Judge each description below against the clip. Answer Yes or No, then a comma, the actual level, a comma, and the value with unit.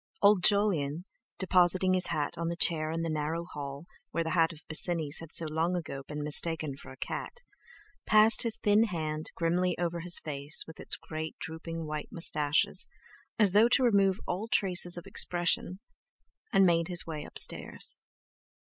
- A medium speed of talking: Yes, average, 170 wpm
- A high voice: No, medium, 170 Hz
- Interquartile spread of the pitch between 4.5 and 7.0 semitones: No, average, 3.0 semitones